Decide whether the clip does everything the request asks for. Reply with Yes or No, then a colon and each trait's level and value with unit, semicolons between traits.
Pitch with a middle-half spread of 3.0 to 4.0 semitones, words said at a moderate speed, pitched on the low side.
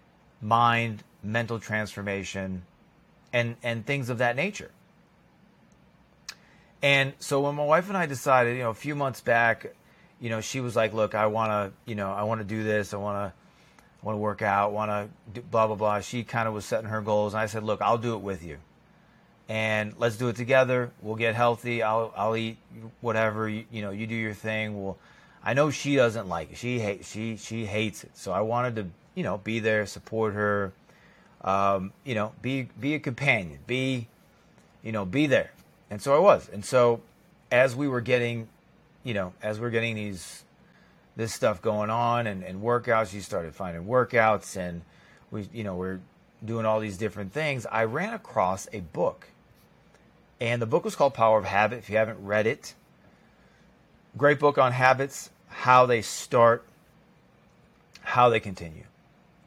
No: narrow, 2.6 semitones; average, 185 wpm; low, 110 Hz